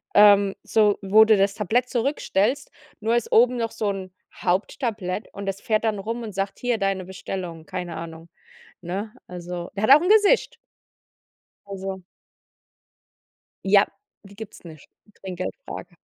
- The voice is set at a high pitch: Yes, high, 200 Hz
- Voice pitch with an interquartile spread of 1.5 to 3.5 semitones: Yes, average, 3.1 semitones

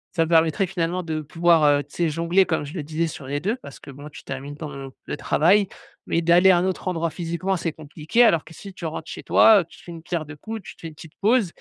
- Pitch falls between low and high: Yes, medium, 165 Hz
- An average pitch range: Yes, average, 3.1 semitones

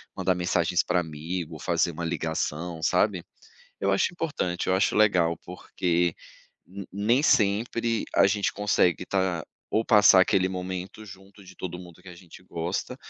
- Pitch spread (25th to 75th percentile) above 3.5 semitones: No, narrow, 2.4 semitones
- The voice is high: No, very low, 90 Hz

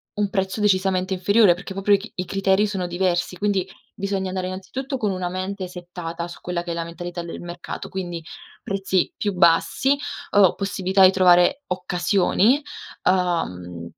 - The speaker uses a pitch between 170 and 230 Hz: Yes, medium, 185 Hz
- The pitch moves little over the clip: Yes, narrow, 2.0 semitones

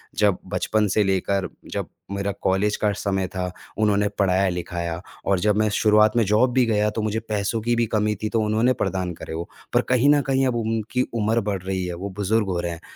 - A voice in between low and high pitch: No, low, 105 Hz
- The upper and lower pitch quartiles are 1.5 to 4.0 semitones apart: Yes, average, 2.7 semitones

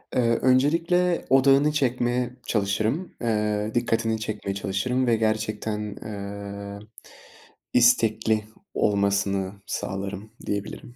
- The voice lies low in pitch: Yes, low, 110 Hz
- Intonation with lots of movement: No, average, 3.6 semitones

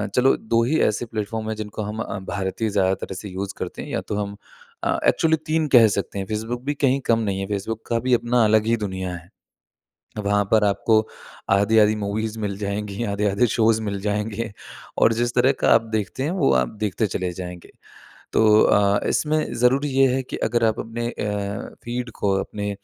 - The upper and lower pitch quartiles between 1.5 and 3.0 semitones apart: Yes, average, 2.7 semitones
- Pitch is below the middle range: Yes, low, 110 Hz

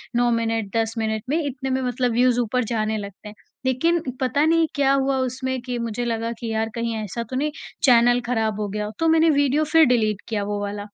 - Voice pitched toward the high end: Yes, high, 240 Hz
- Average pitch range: Yes, average, 3.2 semitones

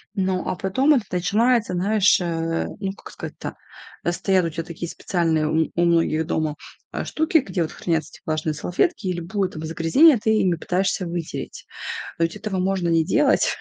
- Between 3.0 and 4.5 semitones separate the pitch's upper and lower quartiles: Yes, average, 3.6 semitones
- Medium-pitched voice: Yes, medium, 180 Hz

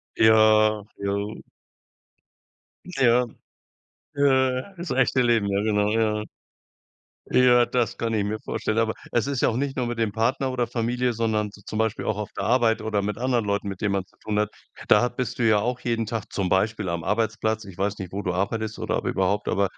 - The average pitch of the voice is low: Yes, low, 110 Hz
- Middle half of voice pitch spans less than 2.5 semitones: No, average, 2.8 semitones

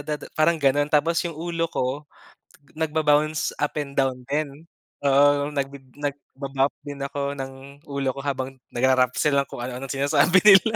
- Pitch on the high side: No, medium, 140 Hz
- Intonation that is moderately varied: No, narrow, 1.8 semitones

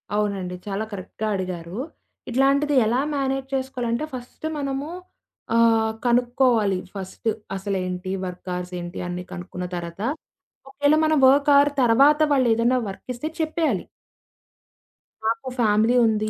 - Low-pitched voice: No, high, 230 Hz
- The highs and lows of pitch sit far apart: Yes, wide, 6.0 semitones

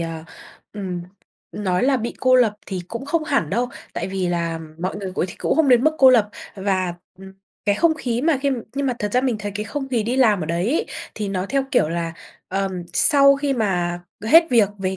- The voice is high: Yes, high, 210 Hz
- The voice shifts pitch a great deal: Yes, wide, 6.0 semitones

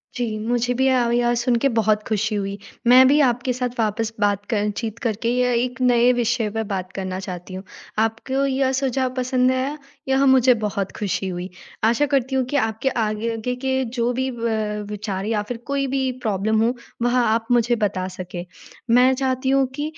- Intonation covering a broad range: No, average, 3.4 semitones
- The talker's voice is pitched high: Yes, high, 240 Hz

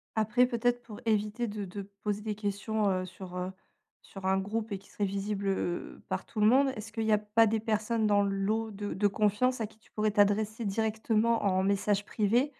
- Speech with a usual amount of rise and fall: No, narrow, 1.9 semitones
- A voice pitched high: Yes, high, 210 Hz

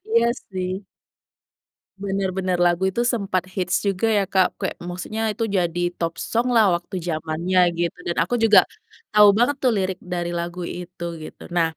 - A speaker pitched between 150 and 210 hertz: Yes, medium, 185 Hz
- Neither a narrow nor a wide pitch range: Yes, average, 3.3 semitones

